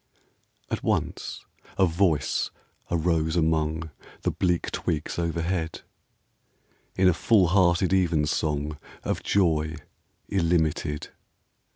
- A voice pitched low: Yes, very low, 80 Hz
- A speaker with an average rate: No, slow, 90 wpm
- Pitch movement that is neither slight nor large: No, narrow, 2.3 semitones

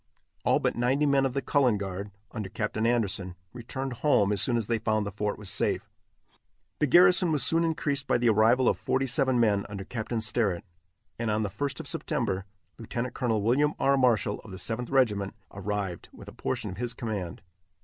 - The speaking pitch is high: No, low, 115 Hz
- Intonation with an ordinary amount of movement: Yes, average, 4.5 semitones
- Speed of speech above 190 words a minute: Yes, average, 200 wpm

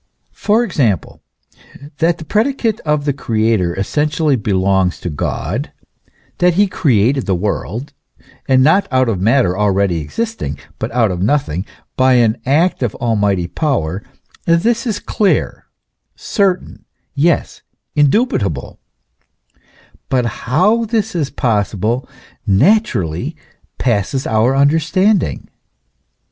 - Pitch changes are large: Yes, wide, 8.7 semitones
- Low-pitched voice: Yes, low, 130 Hz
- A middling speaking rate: No, slow, 110 wpm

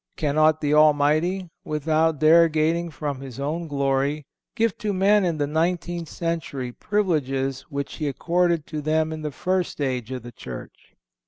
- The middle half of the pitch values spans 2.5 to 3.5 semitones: Yes, average, 3.1 semitones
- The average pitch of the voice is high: No, medium, 155 Hz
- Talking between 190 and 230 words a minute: No, average, 155 wpm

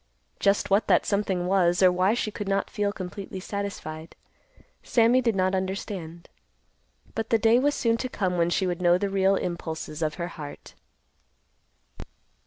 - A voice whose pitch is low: No, high, 190 Hz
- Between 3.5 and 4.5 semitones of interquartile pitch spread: No, average, 2.7 semitones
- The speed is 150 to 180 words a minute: Yes, average, 165 wpm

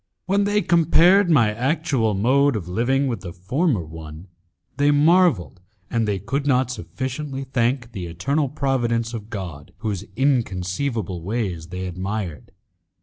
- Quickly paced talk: No, average, 140 wpm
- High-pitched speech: No, low, 115 Hz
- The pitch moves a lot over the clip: Yes, wide, 7.2 semitones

